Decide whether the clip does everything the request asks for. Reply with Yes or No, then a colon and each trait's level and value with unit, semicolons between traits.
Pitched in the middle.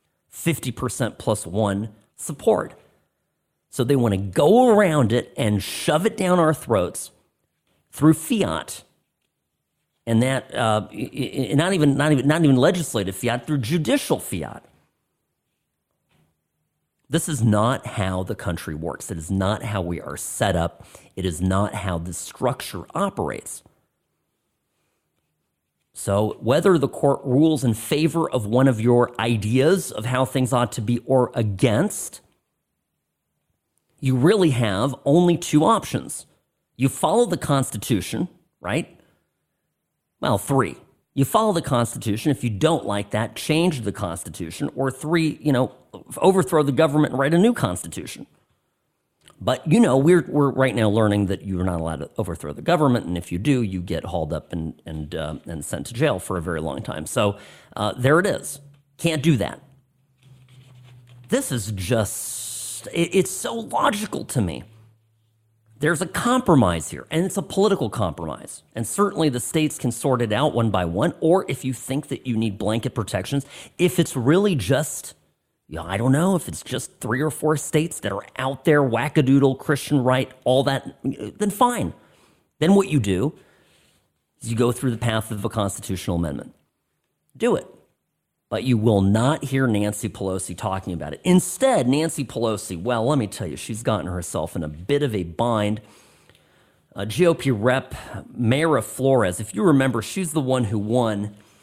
No: low, 125 Hz